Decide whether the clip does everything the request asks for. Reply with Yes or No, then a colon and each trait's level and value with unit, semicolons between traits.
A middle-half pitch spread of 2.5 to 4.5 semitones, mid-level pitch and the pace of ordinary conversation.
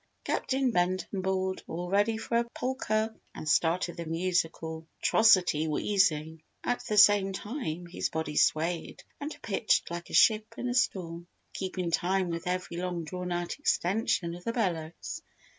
Yes: average, 3.8 semitones; medium, 180 Hz; average, 155 wpm